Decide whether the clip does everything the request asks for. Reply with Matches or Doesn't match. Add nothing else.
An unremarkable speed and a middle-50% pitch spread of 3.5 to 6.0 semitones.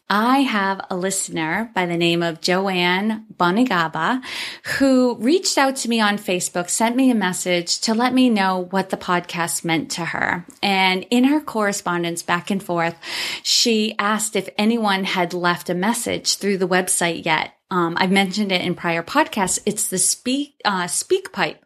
Matches